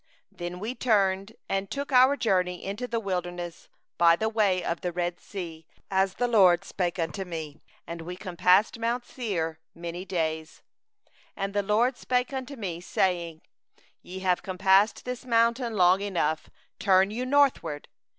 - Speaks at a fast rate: No, average, 155 wpm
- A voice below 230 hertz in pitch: Yes, high, 190 Hz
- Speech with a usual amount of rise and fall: Yes, average, 4.6 semitones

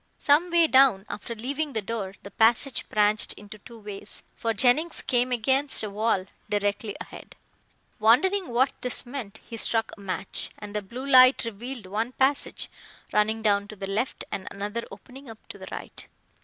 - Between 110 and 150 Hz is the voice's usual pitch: No, high, 225 Hz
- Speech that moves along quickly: No, average, 175 wpm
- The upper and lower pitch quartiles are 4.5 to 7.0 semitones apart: No, average, 4.0 semitones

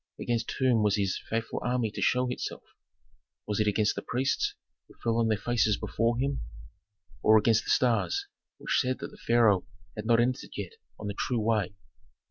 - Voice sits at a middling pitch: No, low, 115 Hz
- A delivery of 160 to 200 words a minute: Yes, average, 185 wpm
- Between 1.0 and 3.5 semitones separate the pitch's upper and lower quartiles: Yes, narrow, 2.5 semitones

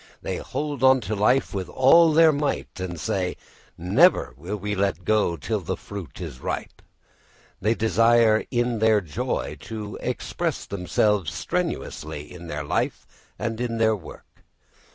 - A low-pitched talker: Yes, low, 105 Hz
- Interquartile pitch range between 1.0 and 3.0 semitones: No, average, 4.9 semitones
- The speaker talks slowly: No, average, 150 wpm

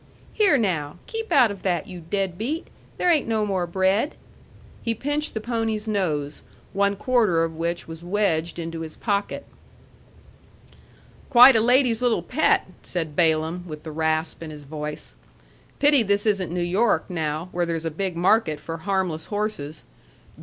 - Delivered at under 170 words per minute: Yes, average, 160 wpm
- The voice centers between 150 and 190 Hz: Yes, medium, 185 Hz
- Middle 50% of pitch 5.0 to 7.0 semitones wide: Yes, average, 5.3 semitones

